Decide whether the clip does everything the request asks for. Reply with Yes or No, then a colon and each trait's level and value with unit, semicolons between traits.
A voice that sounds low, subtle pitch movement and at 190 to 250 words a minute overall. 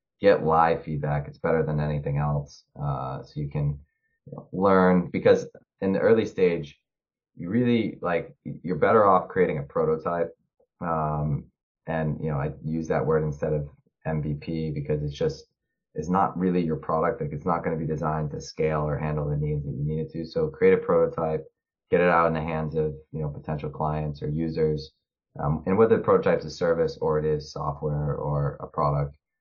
Yes: very low, 75 Hz; narrow, 1.8 semitones; average, 200 wpm